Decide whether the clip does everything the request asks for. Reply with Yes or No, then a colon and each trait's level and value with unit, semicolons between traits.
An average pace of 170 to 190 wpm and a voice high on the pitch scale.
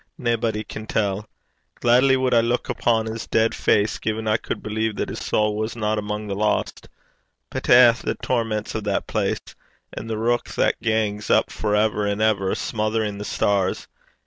No: average, 180 wpm; low, 110 Hz